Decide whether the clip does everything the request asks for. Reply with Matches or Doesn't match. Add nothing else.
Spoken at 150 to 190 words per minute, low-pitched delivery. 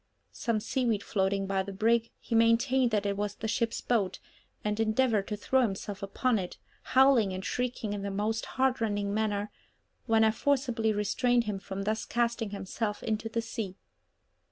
Doesn't match